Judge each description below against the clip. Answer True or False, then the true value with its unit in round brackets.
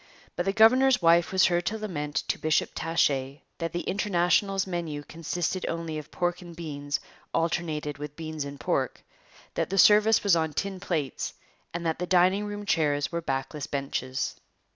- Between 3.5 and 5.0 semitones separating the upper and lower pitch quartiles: True (4.0 semitones)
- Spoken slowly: False (170 wpm)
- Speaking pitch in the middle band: True (170 Hz)